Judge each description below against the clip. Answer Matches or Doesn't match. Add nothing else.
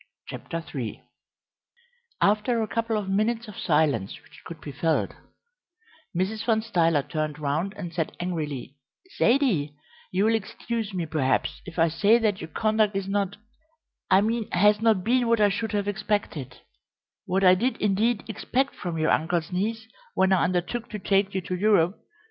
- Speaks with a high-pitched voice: Matches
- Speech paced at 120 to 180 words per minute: Matches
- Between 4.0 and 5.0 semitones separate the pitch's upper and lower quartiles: Matches